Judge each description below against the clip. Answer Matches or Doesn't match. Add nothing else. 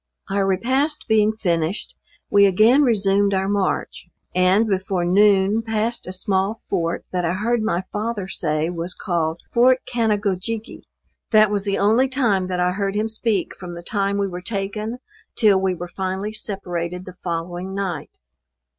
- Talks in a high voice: Matches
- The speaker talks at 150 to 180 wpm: Matches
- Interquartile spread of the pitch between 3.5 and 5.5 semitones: Doesn't match